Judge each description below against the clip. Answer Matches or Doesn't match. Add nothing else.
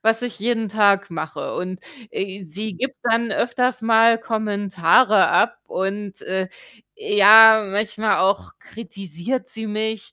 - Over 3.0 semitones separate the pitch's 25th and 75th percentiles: Doesn't match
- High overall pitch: Matches